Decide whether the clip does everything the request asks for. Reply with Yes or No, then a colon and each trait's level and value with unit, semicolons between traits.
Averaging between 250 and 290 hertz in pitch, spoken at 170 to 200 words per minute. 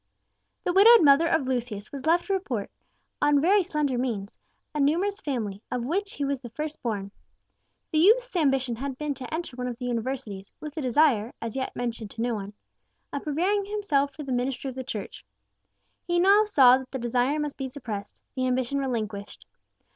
Yes: very high, 270 Hz; average, 190 wpm